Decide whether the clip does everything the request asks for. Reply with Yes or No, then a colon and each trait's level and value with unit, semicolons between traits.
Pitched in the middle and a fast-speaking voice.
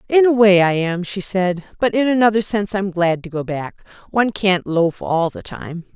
No: high, 195 Hz; fast, 220 wpm